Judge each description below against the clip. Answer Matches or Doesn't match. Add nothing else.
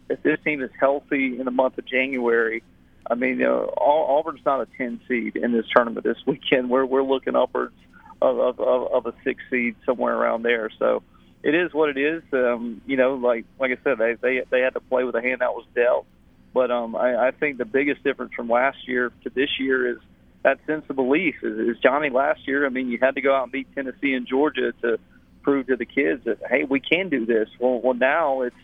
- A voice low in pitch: Matches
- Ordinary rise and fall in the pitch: Doesn't match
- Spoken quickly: Matches